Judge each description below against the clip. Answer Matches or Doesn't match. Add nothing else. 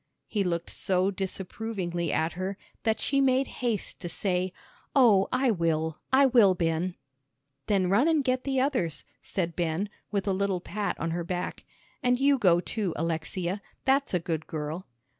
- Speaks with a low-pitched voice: Doesn't match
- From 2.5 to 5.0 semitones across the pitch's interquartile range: Doesn't match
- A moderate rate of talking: Matches